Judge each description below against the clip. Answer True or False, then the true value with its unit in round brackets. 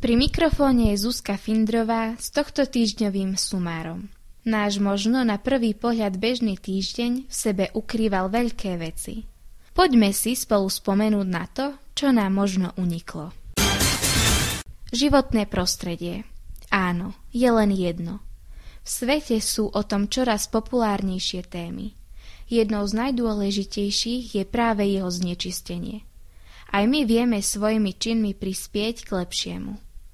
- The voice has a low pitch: False (210 Hz)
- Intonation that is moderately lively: True (3.5 semitones)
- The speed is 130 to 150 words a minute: False (120 wpm)